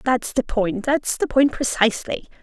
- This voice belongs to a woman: Yes, female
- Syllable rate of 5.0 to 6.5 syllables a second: No, 4.8 syllables/s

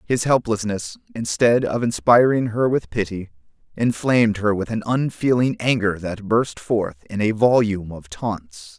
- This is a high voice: No, low, 110 Hz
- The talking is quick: No, average, 150 wpm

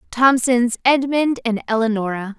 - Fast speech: No, slow, 100 wpm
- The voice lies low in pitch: No, high, 240 Hz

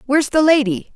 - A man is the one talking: No, female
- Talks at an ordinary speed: Yes, average, 190 wpm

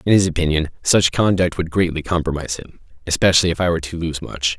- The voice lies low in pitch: Yes, very low, 85 Hz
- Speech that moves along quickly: No, average, 195 wpm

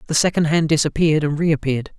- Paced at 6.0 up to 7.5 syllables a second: Yes, 6.7 syllables/s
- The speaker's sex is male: Yes, male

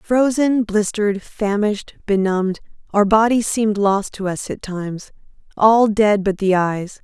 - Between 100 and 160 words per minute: Yes, slow, 135 wpm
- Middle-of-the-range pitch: No, high, 205 Hz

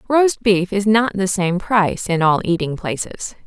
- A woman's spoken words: Yes, female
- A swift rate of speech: No, average, 190 wpm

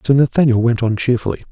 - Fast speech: No, average, 195 wpm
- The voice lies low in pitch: Yes, low, 120 Hz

